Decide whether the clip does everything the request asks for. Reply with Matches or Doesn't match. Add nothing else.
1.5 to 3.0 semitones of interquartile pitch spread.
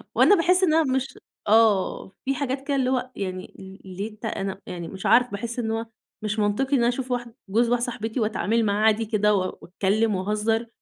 Doesn't match